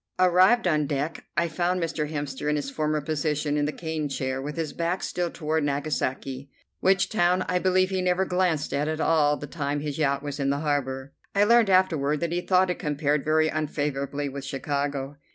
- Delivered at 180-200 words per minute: Yes, average, 190 wpm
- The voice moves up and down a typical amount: Yes, average, 3.4 semitones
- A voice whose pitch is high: No, medium, 150 Hz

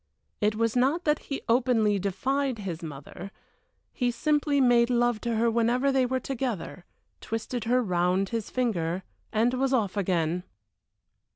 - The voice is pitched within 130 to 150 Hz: No, high, 230 Hz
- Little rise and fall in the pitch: No, average, 4.4 semitones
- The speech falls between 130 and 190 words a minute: Yes, average, 150 wpm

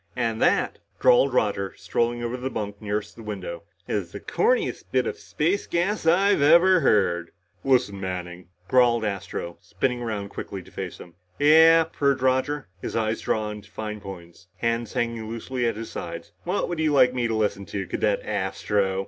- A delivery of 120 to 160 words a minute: No, average, 175 wpm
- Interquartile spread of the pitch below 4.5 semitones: No, average, 4.9 semitones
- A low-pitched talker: Yes, low, 115 Hz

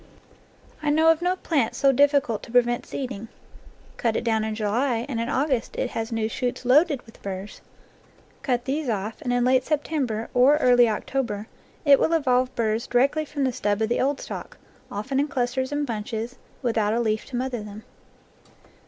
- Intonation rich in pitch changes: No, average, 3.7 semitones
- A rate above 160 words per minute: Yes, average, 190 wpm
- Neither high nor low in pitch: No, high, 245 Hz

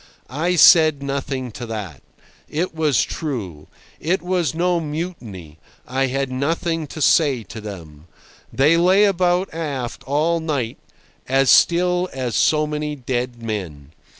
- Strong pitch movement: Yes, wide, 5.7 semitones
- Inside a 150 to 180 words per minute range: No, slow, 135 wpm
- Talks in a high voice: No, medium, 140 Hz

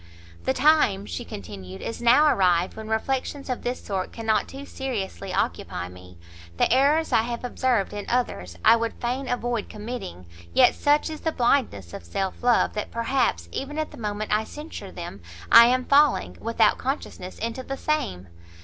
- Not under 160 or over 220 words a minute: Yes, average, 175 wpm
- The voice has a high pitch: Yes, high, 230 Hz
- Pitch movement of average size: No, wide, 6.0 semitones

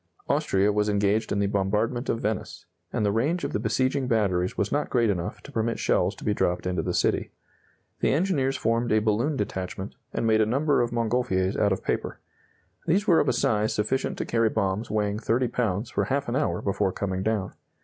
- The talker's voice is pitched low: Yes, low, 110 Hz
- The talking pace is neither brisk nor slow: No, fast, 210 wpm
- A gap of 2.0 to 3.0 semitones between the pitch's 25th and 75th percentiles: No, average, 3.6 semitones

